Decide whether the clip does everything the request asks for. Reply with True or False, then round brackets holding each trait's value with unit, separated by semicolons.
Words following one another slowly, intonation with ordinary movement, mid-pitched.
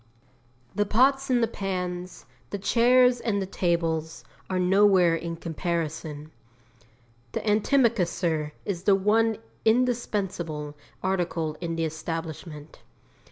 True (110 wpm; 4.4 semitones; 180 Hz)